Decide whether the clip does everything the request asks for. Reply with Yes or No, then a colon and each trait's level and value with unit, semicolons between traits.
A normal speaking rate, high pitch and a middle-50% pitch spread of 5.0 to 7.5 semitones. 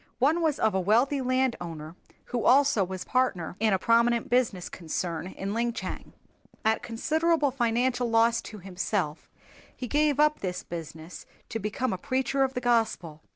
Yes: average, 160 wpm; high, 230 Hz; wide, 5.6 semitones